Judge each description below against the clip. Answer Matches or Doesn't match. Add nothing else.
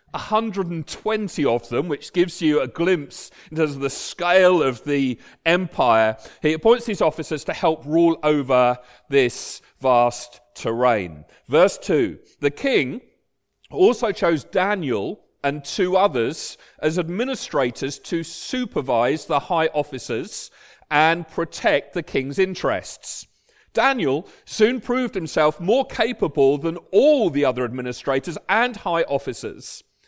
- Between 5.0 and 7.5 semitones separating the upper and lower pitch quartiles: Matches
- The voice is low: Doesn't match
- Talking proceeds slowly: Matches